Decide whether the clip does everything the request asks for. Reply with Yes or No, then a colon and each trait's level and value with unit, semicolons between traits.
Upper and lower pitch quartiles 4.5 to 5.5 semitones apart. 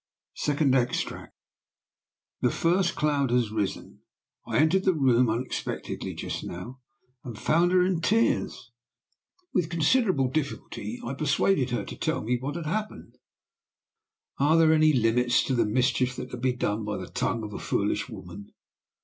Yes: average, 4.9 semitones